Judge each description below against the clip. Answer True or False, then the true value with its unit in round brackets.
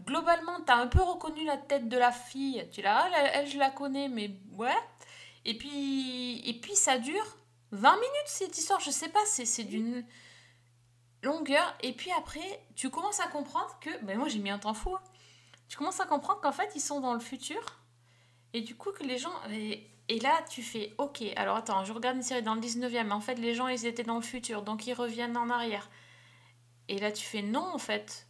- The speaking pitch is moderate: False (250 Hz)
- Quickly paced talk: True (225 wpm)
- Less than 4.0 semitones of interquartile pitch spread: False (5.5 semitones)